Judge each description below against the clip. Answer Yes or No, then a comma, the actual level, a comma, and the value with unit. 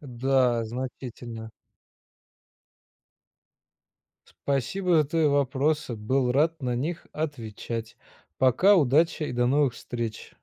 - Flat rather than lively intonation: No, average, 3.9 semitones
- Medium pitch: No, low, 130 Hz